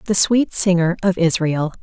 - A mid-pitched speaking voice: Yes, medium, 180 Hz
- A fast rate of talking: No, average, 165 wpm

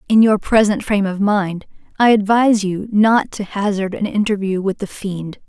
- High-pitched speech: Yes, high, 205 Hz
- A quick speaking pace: No, average, 185 wpm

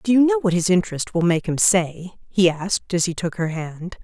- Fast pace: Yes, fast, 255 wpm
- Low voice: No, medium, 185 Hz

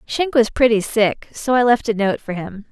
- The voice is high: Yes, high, 225 Hz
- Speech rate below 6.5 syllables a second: Yes, 4.7 syllables/s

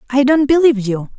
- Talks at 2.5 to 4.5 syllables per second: No, 6.3 syllables/s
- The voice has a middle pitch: No, very high, 255 Hz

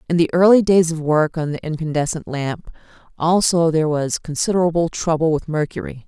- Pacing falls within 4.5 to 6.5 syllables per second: Yes, 5.6 syllables/s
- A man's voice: No, female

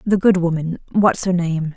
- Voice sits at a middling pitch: Yes, medium, 175 Hz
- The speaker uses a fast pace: No, average, 170 wpm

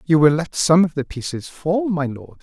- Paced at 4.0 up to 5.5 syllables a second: Yes, 5.0 syllables/s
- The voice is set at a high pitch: No, medium, 155 Hz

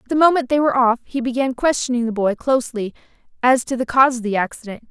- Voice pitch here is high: Yes, very high, 250 Hz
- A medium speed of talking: No, fast, 220 wpm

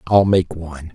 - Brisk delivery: No, average, 190 wpm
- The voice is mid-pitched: No, very low, 85 Hz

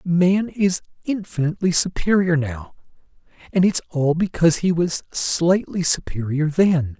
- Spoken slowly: Yes, slow, 120 wpm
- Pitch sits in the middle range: Yes, medium, 170 Hz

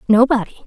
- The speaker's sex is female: Yes, female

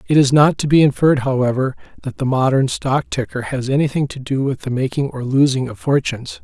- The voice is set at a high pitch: No, low, 135 Hz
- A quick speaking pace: Yes, fast, 215 wpm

